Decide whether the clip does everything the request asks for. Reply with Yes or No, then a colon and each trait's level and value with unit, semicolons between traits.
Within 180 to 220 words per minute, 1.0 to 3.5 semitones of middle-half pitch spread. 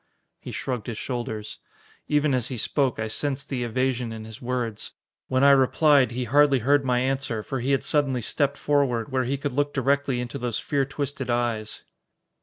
Yes: average, 190 wpm; average, 2.7 semitones